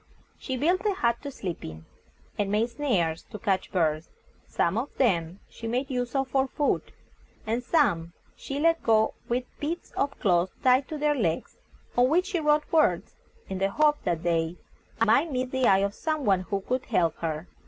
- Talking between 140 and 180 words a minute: No, average, 190 wpm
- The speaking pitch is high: Yes, high, 235 Hz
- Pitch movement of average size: No, wide, 7.4 semitones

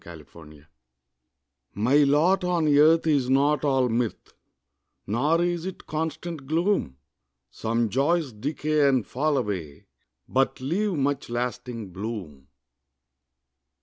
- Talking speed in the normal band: No, slow, 115 wpm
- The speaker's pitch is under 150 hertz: Yes, low, 135 Hz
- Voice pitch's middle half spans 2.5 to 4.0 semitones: No, wide, 5.6 semitones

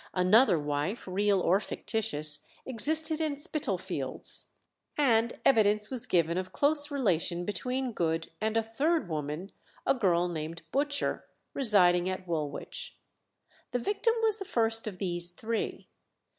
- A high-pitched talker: Yes, high, 215 Hz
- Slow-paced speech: Yes, slow, 130 wpm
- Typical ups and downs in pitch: No, wide, 7.5 semitones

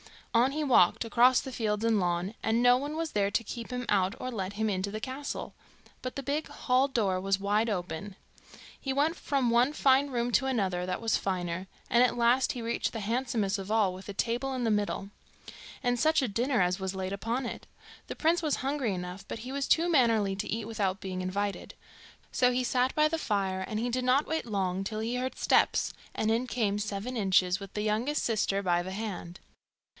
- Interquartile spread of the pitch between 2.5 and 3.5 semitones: No, average, 4.4 semitones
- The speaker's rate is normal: No, fast, 215 wpm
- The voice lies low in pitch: No, high, 225 Hz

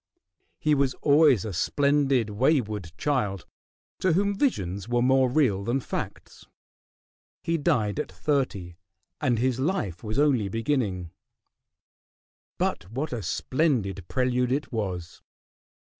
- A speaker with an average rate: No, slow, 120 wpm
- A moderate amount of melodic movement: No, wide, 6.1 semitones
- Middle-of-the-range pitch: No, low, 125 Hz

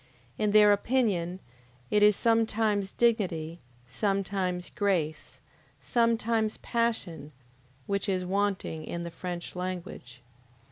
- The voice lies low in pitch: No, high, 195 Hz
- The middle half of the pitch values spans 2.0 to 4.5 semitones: Yes, average, 3.7 semitones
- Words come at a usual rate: No, slow, 100 wpm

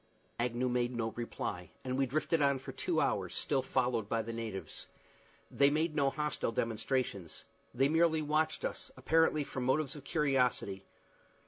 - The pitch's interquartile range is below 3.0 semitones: No, average, 4.4 semitones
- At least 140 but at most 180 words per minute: Yes, average, 155 wpm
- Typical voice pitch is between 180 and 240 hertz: No, low, 130 Hz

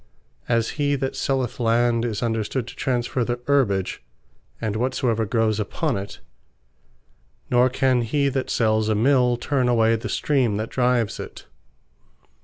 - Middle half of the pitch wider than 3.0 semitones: No, narrow, 2.5 semitones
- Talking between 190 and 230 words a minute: No, average, 145 wpm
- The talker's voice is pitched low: Yes, low, 120 Hz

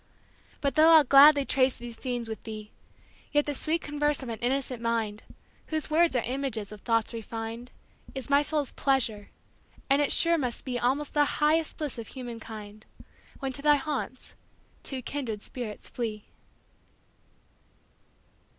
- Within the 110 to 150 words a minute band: Yes, average, 140 wpm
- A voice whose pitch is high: Yes, very high, 260 Hz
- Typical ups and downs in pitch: Yes, average, 4.3 semitones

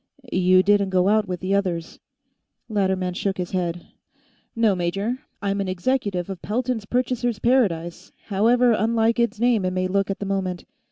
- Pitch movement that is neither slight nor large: Yes, average, 3.6 semitones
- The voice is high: Yes, high, 200 Hz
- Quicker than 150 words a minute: Yes, average, 165 wpm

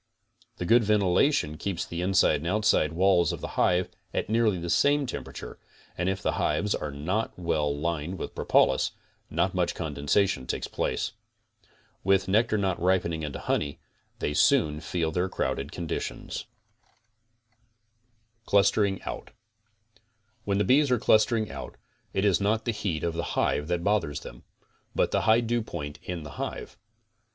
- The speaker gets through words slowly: No, average, 155 wpm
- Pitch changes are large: No, average, 4.6 semitones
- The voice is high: No, very low, 90 Hz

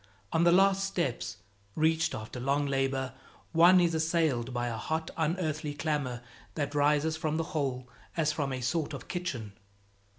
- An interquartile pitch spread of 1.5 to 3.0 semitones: No, average, 3.6 semitones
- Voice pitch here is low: No, medium, 150 Hz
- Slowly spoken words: No, average, 160 wpm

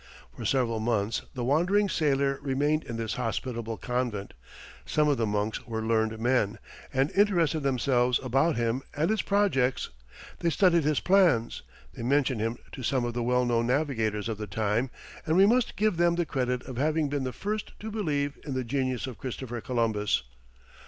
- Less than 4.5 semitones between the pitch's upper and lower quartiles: No, average, 4.8 semitones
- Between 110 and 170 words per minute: No, average, 180 wpm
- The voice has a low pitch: Yes, low, 130 Hz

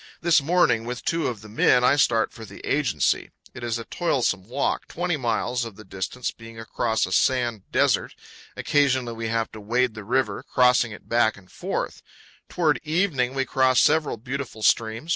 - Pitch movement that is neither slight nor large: Yes, average, 3.6 semitones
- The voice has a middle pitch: No, low, 120 Hz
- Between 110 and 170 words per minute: No, average, 195 wpm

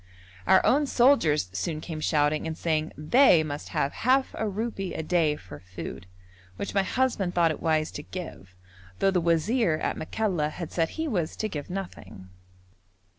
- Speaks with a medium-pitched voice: Yes, medium, 165 Hz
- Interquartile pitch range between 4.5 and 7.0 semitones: Yes, average, 4.9 semitones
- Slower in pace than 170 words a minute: No, average, 175 wpm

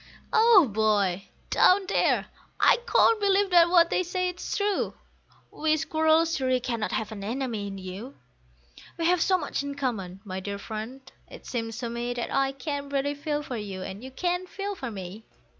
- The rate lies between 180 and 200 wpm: Yes, average, 185 wpm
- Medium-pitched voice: No, very high, 270 Hz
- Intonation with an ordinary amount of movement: No, wide, 7.6 semitones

